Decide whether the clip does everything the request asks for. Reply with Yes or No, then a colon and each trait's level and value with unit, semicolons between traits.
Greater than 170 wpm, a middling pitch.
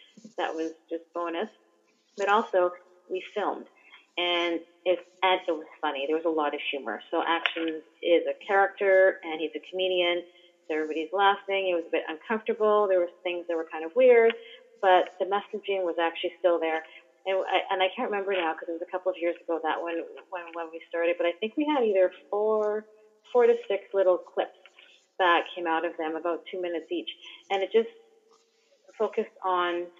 Yes: average, 200 wpm; medium, 180 Hz